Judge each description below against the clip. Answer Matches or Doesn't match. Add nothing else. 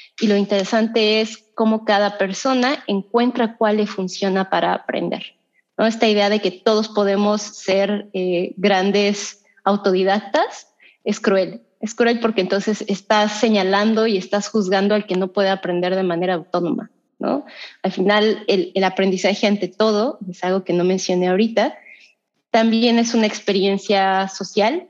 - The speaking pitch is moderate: Doesn't match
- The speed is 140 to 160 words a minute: Matches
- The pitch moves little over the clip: Matches